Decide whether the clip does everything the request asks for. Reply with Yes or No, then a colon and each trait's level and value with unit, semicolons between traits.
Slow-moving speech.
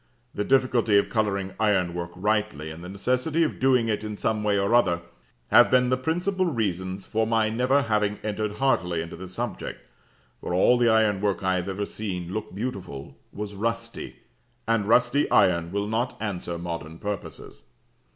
No: average, 170 wpm